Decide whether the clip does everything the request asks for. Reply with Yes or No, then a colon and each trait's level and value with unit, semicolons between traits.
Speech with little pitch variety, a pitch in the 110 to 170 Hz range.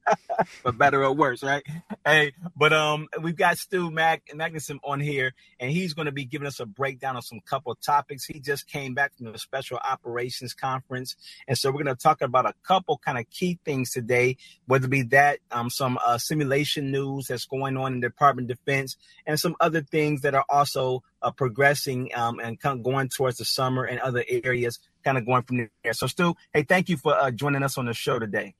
No: average, 3.1 semitones; low, 135 Hz